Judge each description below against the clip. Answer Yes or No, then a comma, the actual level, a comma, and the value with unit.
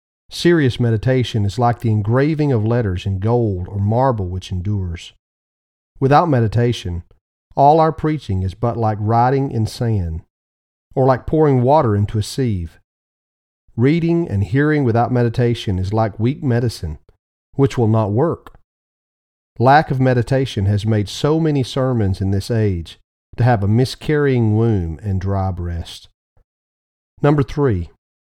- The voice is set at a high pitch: No, low, 110 Hz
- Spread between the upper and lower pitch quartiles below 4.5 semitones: No, wide, 5.5 semitones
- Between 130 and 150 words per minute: Yes, average, 140 wpm